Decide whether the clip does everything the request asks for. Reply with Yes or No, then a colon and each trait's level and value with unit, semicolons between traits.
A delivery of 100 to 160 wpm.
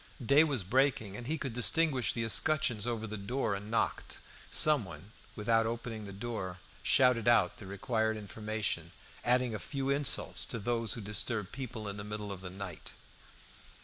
No: average, 170 wpm